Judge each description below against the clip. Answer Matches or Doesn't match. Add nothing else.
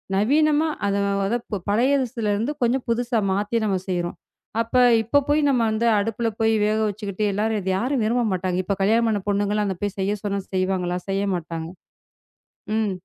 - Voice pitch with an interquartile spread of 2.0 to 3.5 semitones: Matches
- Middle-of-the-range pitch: Doesn't match